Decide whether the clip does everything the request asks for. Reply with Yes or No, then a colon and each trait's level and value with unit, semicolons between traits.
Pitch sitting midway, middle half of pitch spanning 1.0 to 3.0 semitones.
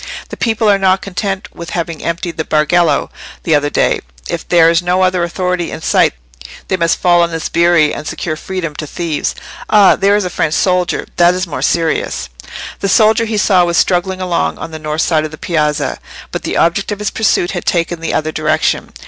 Yes: medium, 175 Hz; narrow, 2.6 semitones